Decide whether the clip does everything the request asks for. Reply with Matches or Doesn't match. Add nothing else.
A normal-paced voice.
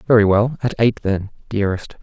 Matches